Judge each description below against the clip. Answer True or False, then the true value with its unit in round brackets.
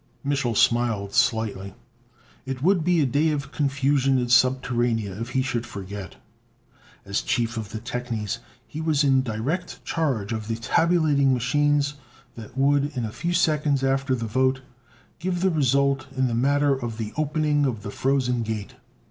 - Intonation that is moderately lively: True (3.8 semitones)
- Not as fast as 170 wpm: True (160 wpm)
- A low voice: True (130 Hz)